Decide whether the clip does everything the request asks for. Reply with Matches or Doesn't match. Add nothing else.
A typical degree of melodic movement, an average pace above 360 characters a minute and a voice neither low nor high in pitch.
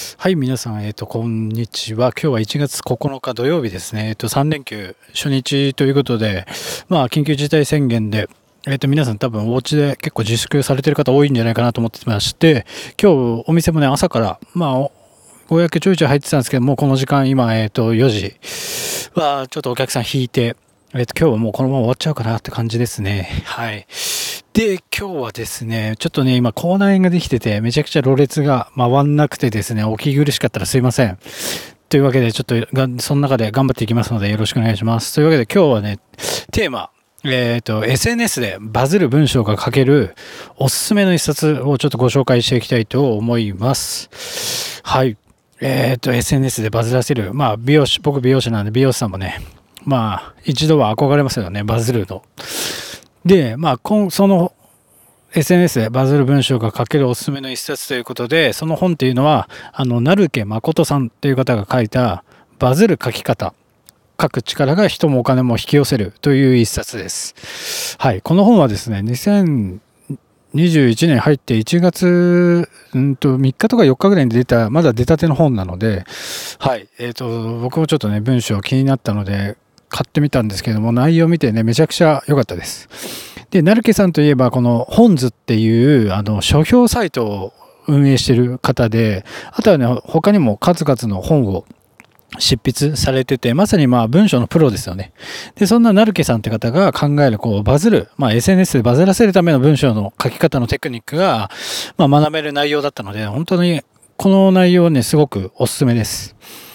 Doesn't match